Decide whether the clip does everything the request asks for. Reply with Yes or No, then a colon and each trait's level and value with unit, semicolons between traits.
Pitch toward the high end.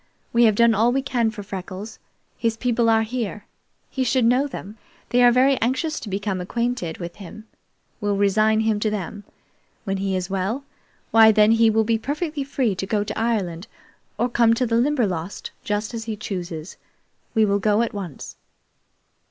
Yes: high, 220 Hz